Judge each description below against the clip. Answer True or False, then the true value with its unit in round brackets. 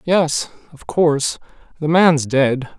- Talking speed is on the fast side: False (130 wpm)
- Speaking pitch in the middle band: True (150 Hz)